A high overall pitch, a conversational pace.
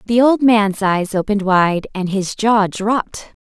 Yes: high, 205 Hz; average, 175 wpm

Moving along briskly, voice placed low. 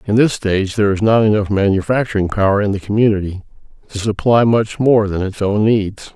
No: average, 195 wpm; low, 105 Hz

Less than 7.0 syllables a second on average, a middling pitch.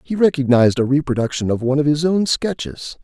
Yes: 6.2 syllables/s; medium, 145 Hz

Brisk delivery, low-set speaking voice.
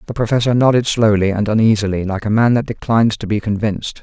Yes: fast, 210 wpm; low, 110 Hz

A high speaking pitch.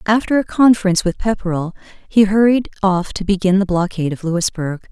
Yes: high, 195 Hz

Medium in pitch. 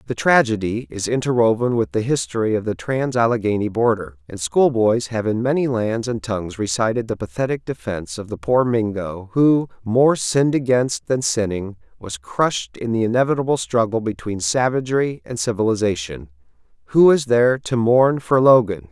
No: low, 115 Hz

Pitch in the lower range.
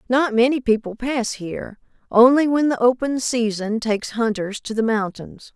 No: high, 235 Hz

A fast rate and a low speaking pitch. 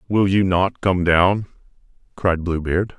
No: average, 160 wpm; very low, 90 Hz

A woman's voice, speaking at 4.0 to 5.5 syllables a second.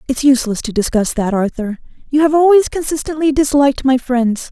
No: female; 5.7 syllables/s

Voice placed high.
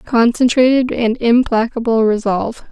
Yes: high, 235 Hz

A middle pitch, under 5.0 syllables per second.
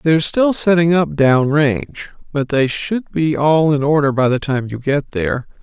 Yes: medium, 145 Hz; 4.6 syllables/s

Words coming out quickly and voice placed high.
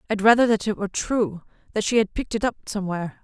Yes: fast, 220 wpm; high, 210 Hz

